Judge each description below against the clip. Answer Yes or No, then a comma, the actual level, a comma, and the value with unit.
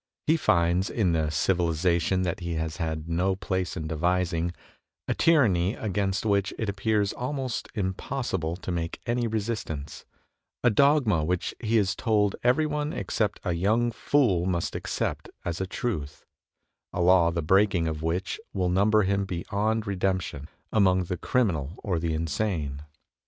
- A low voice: Yes, very low, 95 Hz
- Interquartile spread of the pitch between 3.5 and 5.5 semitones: Yes, average, 4.3 semitones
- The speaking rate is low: No, average, 155 wpm